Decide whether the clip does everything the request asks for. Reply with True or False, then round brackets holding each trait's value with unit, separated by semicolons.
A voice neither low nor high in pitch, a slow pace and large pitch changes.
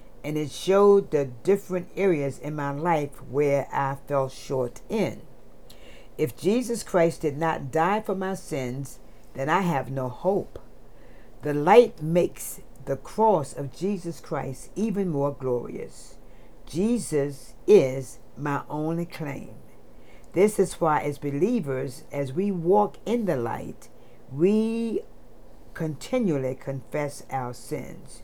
True (150 Hz; 130 wpm; 5.7 semitones)